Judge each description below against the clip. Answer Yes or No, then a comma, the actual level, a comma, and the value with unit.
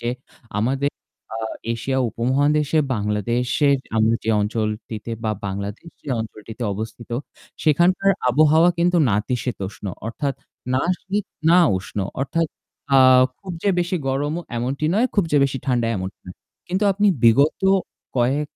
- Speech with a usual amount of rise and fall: No, wide, 6.0 semitones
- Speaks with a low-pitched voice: Yes, low, 130 Hz